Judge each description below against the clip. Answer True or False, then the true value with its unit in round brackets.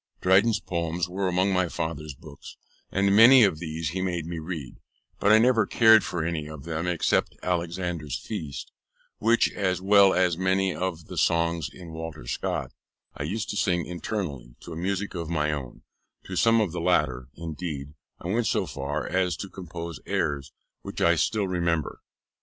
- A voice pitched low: True (85 Hz)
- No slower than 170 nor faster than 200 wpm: True (175 wpm)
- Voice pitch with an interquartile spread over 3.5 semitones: False (3.2 semitones)